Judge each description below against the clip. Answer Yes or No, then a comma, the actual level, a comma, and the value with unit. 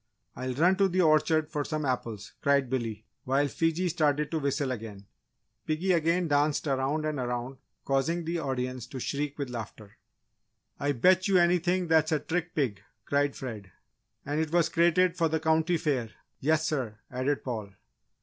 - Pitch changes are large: No, average, 4.1 semitones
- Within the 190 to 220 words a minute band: No, average, 170 wpm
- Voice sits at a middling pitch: Yes, medium, 145 Hz